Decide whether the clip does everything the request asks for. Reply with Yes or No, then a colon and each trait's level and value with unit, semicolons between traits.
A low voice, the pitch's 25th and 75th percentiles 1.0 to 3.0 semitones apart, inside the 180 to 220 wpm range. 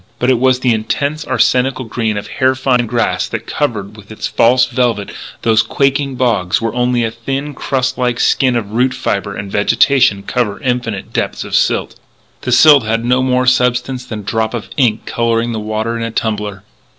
Yes: low, 120 Hz; average, 2.7 semitones; average, 190 wpm